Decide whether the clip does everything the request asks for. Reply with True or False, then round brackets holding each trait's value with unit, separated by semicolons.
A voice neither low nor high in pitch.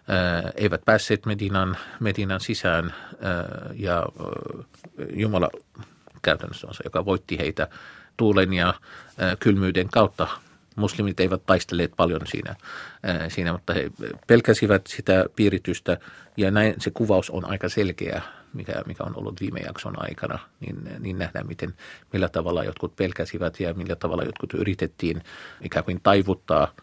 False (95 Hz)